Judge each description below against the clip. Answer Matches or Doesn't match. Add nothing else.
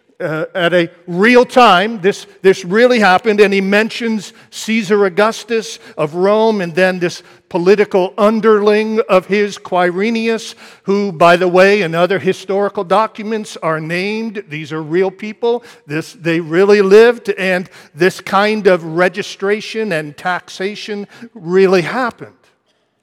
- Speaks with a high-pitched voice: Matches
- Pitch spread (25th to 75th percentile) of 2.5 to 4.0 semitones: Matches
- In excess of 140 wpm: Doesn't match